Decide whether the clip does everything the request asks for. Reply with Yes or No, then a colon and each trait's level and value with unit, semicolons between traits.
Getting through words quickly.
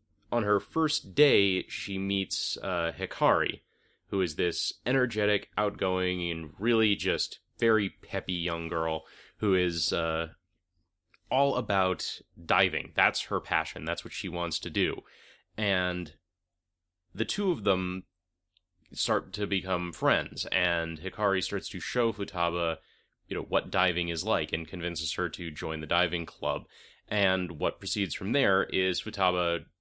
No: average, 145 wpm